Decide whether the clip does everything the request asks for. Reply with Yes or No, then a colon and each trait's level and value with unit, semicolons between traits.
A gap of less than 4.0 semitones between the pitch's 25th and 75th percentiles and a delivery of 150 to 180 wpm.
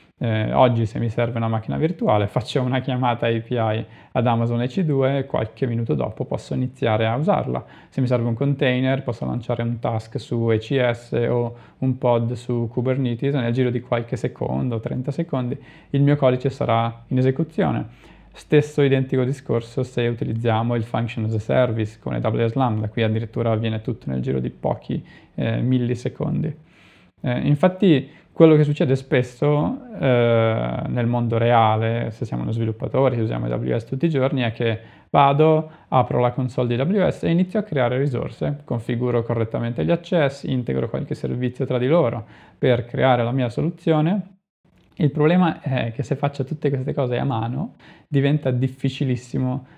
Yes: average, 3.3 semitones; average, 165 wpm